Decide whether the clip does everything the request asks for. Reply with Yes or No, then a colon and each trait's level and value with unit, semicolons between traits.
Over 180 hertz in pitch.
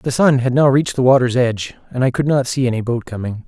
No: low, 125 Hz